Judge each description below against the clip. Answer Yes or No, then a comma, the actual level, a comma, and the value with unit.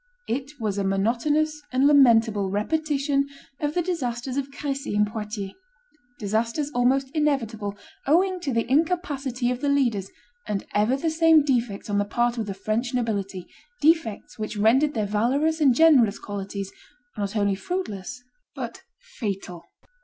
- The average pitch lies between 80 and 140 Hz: No, high, 245 Hz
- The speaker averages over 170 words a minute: No, average, 145 wpm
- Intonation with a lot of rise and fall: Yes, wide, 5.7 semitones